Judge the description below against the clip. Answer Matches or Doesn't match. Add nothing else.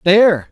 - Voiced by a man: Matches